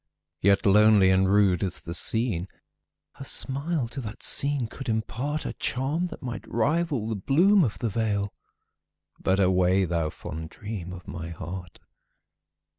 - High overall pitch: No, low, 105 Hz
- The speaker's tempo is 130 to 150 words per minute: Yes, slow, 135 wpm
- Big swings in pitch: Yes, wide, 6.1 semitones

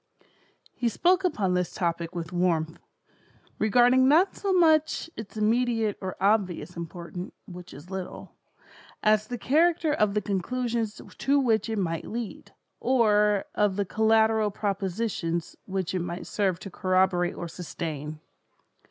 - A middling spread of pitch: Yes, average, 4.6 semitones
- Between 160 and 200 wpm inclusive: No, slow, 135 wpm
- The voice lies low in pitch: No, high, 205 Hz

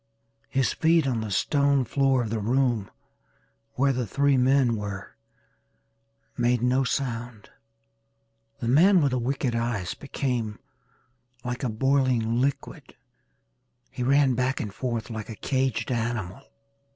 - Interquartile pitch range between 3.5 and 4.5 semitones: No, average, 2.9 semitones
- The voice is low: Yes, low, 125 Hz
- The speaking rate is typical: No, slow, 130 wpm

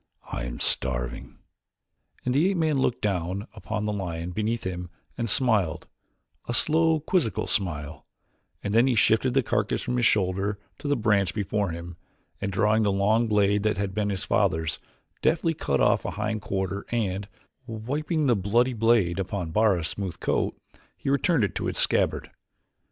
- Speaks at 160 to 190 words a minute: Yes, average, 170 wpm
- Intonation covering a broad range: No, average, 4.0 semitones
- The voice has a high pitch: No, low, 105 Hz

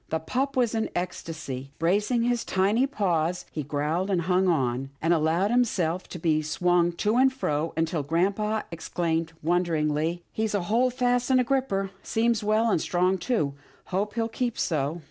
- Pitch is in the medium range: Yes, medium, 180 Hz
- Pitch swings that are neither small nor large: No, wide, 5.7 semitones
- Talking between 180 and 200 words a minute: Yes, average, 185 wpm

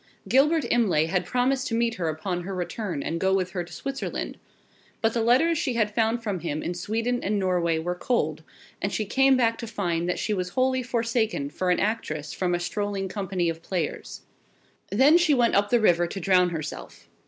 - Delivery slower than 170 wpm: No, average, 200 wpm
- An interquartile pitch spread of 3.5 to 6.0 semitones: Yes, average, 5.0 semitones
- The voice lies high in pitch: Yes, high, 200 Hz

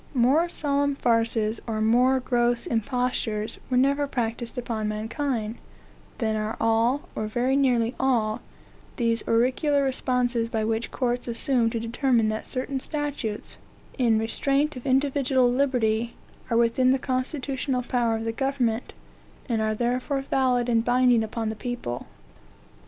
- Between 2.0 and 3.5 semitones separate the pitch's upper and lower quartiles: Yes, average, 2.8 semitones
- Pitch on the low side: No, high, 245 Hz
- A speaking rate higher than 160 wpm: No, average, 140 wpm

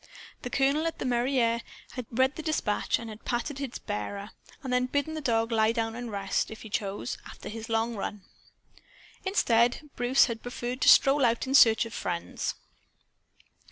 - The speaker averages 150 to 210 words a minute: Yes, average, 180 wpm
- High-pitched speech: Yes, high, 235 Hz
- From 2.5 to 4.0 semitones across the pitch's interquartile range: Yes, average, 2.8 semitones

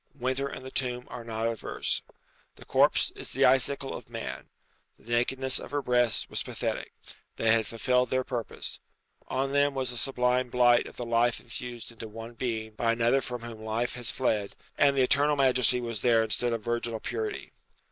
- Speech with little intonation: Yes, narrow, 2.0 semitones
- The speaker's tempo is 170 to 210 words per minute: Yes, average, 185 wpm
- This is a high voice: No, low, 120 Hz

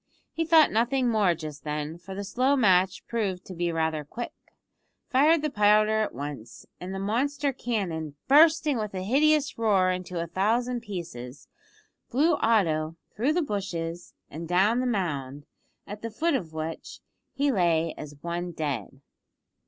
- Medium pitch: No, high, 195 Hz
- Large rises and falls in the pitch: Yes, wide, 6.9 semitones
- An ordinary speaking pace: Yes, average, 160 wpm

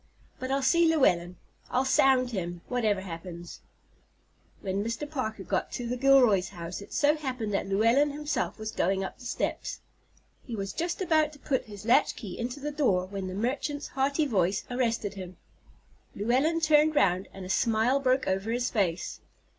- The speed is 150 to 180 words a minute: Yes, average, 170 wpm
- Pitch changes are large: Yes, wide, 6.0 semitones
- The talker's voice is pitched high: Yes, high, 235 Hz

